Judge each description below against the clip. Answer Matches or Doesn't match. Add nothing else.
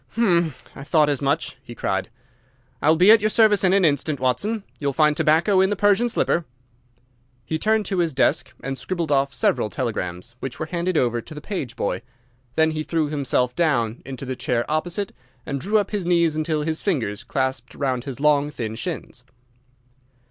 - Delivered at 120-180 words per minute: Doesn't match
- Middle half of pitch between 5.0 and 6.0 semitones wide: Matches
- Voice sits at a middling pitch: Matches